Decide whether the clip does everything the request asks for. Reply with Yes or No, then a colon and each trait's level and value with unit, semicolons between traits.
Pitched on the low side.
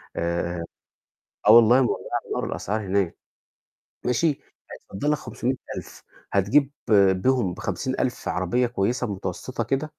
Yes: low, 115 Hz